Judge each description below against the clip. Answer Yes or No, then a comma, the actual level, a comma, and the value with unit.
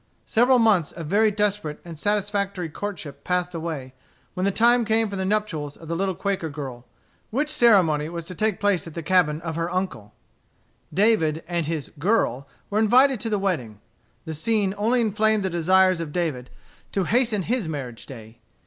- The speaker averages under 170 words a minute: No, average, 180 wpm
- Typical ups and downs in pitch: Yes, average, 4.9 semitones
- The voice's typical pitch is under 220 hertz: Yes, medium, 185 Hz